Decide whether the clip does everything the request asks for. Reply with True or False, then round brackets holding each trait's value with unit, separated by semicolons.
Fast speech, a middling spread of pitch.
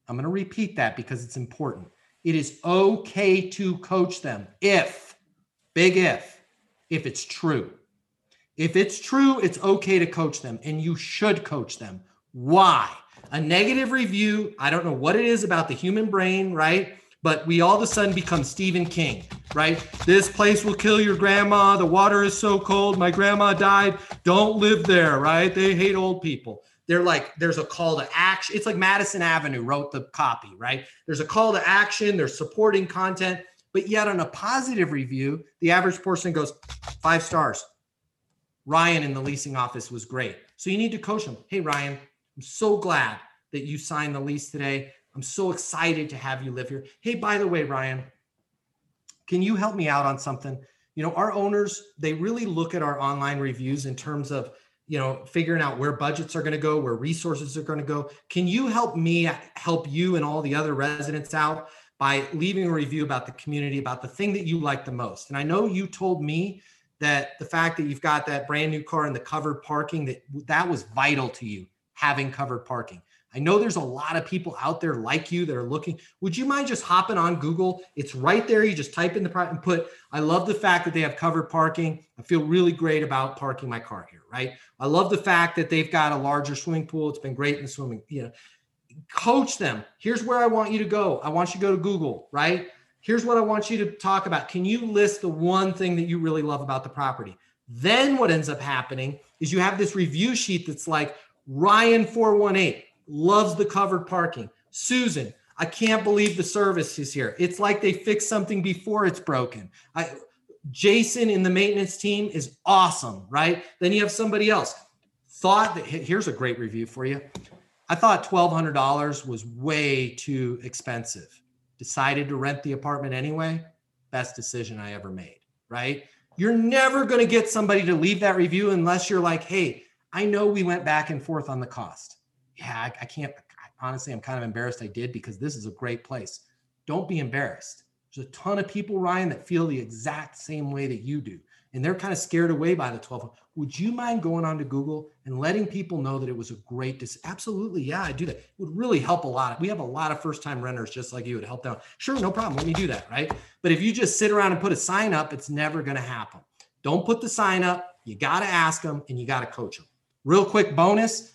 False (215 wpm; 5.7 semitones)